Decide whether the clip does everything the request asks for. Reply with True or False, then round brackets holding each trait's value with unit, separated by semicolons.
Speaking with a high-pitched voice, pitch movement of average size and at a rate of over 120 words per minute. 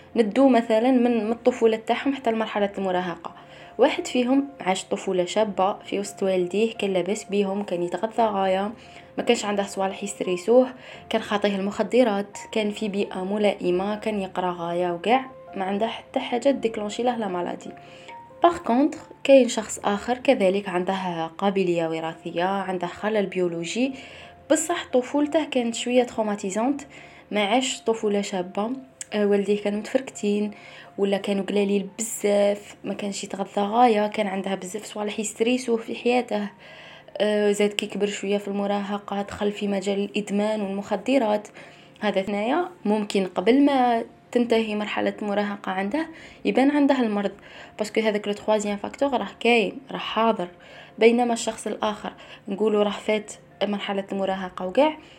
True (210 Hz; 3.0 semitones; 135 wpm)